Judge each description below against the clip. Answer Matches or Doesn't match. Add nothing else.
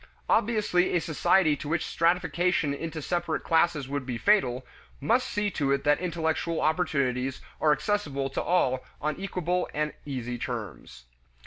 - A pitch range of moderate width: Matches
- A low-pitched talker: Doesn't match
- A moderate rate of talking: Matches